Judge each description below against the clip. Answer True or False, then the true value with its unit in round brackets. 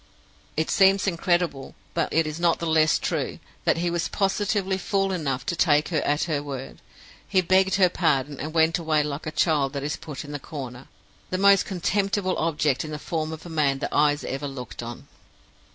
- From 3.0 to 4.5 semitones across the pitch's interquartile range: True (3.7 semitones)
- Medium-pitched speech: True (160 Hz)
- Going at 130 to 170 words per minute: False (200 wpm)